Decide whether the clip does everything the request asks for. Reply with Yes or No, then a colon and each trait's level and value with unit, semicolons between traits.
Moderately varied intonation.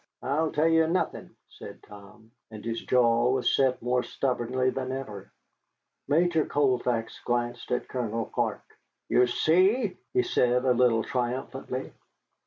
Yes: average, 3.0 semitones